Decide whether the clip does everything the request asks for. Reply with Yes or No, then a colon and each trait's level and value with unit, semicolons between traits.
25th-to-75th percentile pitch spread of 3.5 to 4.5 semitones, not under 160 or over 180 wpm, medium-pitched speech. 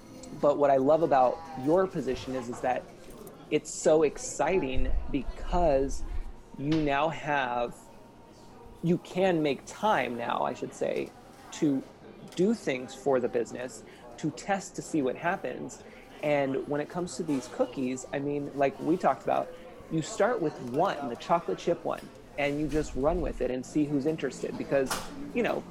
Yes: average, 4.2 semitones; average, 165 wpm; medium, 145 Hz